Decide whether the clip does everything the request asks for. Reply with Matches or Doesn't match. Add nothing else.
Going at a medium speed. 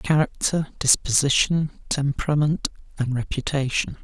Doesn't match